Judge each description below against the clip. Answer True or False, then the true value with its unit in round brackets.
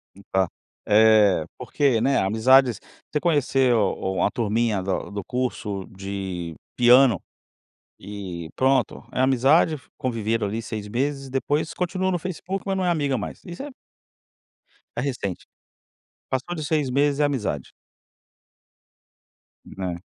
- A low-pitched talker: True (125 Hz)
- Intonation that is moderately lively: False (5.9 semitones)